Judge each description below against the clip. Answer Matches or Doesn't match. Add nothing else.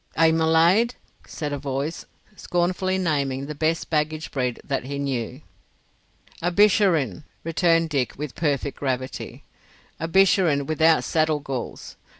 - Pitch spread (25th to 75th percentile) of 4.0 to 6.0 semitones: Doesn't match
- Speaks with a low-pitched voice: Doesn't match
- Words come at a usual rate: Doesn't match